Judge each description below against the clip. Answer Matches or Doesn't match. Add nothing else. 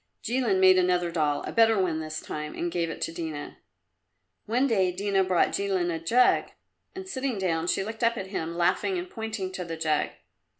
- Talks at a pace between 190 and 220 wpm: Matches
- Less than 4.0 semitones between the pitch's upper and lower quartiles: Doesn't match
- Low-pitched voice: Doesn't match